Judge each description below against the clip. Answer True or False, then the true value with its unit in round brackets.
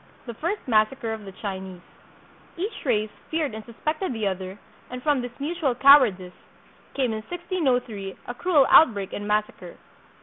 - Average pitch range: False (5.7 semitones)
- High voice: True (240 Hz)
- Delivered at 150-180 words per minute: True (155 wpm)